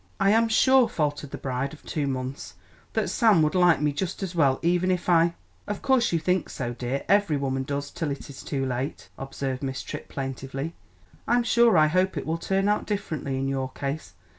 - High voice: No, medium, 155 Hz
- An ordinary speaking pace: No, fast, 215 wpm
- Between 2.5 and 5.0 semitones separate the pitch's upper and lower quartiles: No, wide, 5.6 semitones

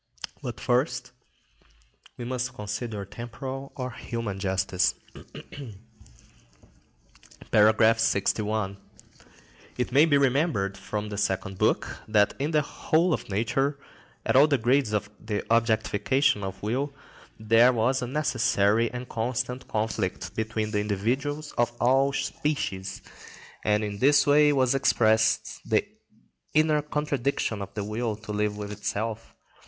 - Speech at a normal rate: No, slow, 125 wpm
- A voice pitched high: No, low, 115 Hz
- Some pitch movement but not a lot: Yes, average, 4.3 semitones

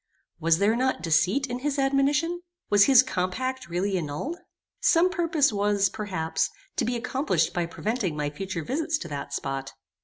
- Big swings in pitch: Yes, wide, 7.9 semitones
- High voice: Yes, high, 220 Hz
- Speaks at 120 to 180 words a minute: Yes, average, 160 wpm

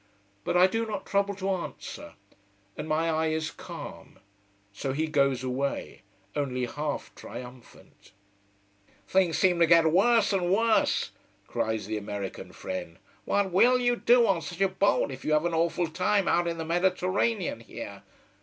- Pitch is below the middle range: No, medium, 170 Hz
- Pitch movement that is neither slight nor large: No, wide, 5.9 semitones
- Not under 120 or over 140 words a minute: No, average, 160 wpm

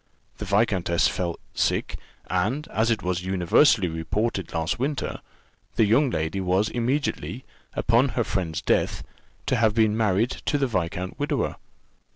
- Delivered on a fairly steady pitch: No, average, 4.6 semitones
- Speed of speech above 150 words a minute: No, average, 145 wpm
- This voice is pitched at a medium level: No, low, 105 Hz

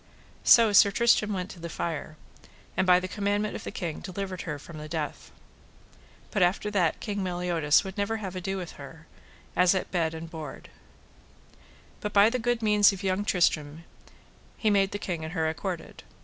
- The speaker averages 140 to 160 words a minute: No, average, 185 wpm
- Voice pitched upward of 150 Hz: Yes, medium, 185 Hz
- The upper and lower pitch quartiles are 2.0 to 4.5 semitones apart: Yes, average, 3.6 semitones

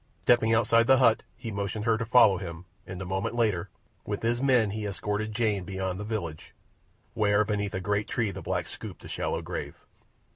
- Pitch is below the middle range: Yes, low, 105 Hz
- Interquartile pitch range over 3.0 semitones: No, average, 2.7 semitones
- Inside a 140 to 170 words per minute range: No, average, 195 wpm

